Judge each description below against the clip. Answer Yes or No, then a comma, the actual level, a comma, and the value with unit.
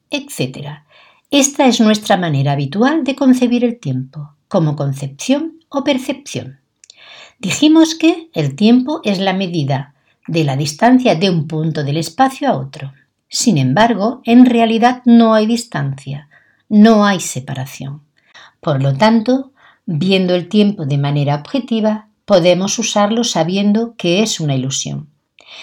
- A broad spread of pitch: Yes, wide, 8.6 semitones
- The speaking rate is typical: Yes, average, 135 wpm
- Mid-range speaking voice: No, high, 200 Hz